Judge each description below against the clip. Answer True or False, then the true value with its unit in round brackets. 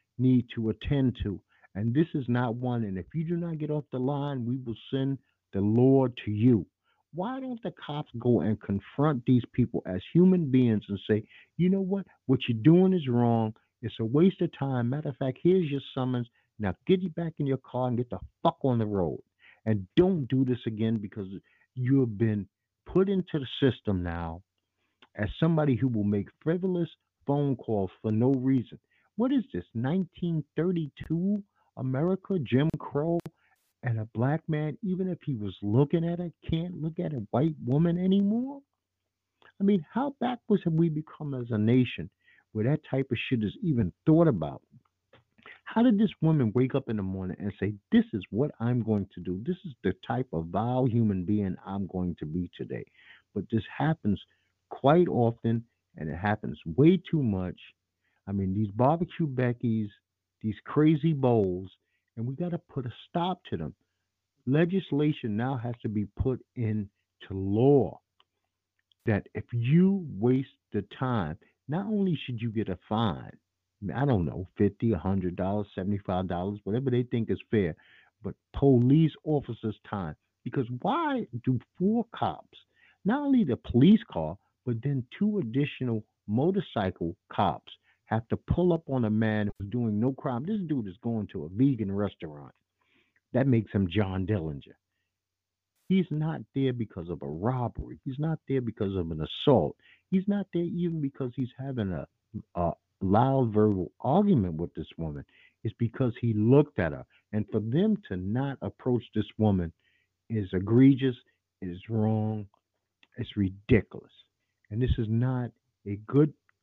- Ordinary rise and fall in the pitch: False (6.5 semitones)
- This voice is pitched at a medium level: False (125 Hz)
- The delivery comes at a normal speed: True (170 wpm)